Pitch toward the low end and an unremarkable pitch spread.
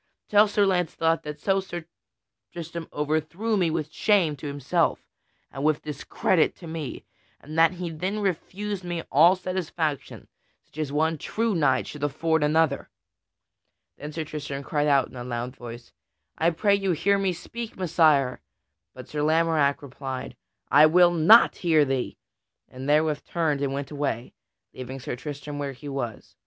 No: medium, 155 Hz; average, 3.5 semitones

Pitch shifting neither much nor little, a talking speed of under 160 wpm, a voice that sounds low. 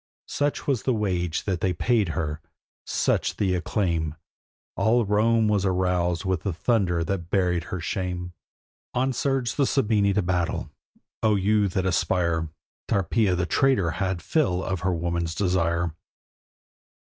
Yes: average, 3.6 semitones; average, 145 wpm; very low, 95 Hz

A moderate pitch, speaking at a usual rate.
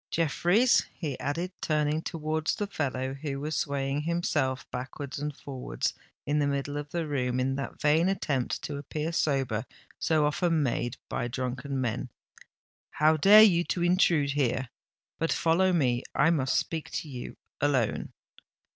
Yes: medium, 145 Hz; average, 150 wpm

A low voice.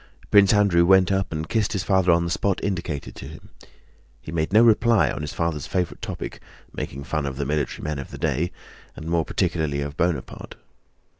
Yes: very low, 85 Hz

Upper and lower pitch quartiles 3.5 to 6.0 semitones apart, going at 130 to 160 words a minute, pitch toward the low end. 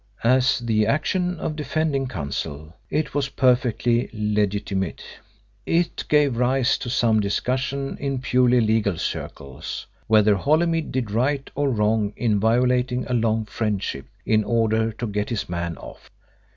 Yes: average, 4.0 semitones; average, 140 wpm; low, 120 Hz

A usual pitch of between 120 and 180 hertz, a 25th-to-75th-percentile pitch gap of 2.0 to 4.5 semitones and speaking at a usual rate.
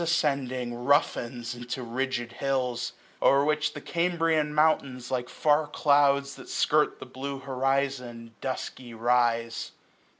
No: low, 135 Hz; average, 3.0 semitones; slow, 120 wpm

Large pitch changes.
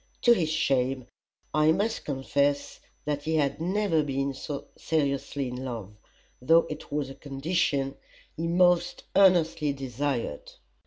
No: average, 3.3 semitones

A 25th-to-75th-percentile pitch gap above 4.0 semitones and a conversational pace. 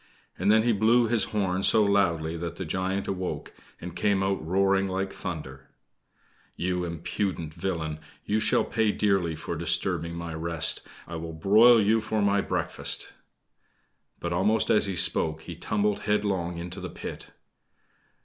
No: average, 3.4 semitones; average, 155 wpm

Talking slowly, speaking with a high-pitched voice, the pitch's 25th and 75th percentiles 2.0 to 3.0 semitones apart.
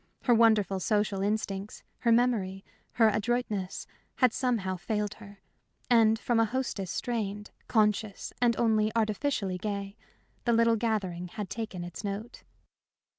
Yes: slow, 130 wpm; high, 215 Hz; average, 2.7 semitones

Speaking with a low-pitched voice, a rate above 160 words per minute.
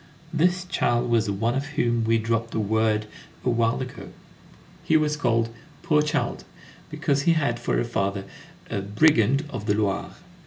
Yes: low, 120 Hz; average, 170 wpm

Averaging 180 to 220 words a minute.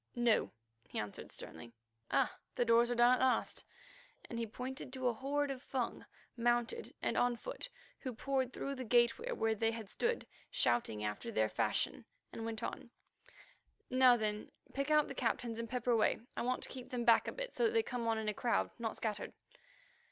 Yes: average, 195 wpm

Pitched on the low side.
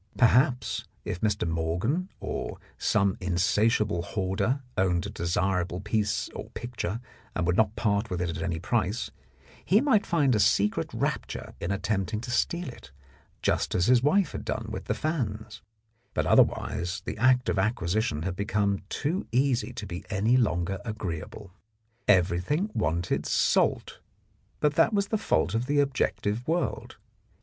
Yes: low, 105 Hz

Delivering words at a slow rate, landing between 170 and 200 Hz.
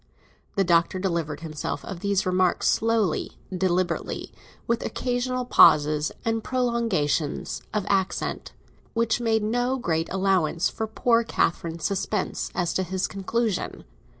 Yes: slow, 125 wpm; high, 190 Hz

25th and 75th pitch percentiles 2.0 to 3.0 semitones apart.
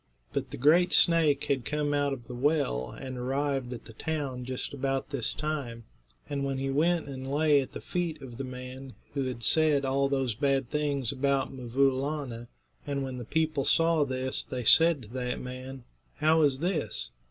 Yes: narrow, 2.6 semitones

